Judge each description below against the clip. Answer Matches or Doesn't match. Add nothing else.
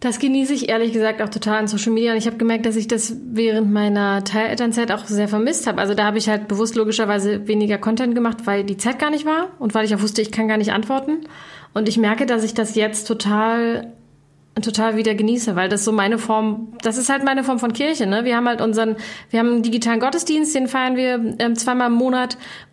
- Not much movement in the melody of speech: Matches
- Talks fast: Matches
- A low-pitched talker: Doesn't match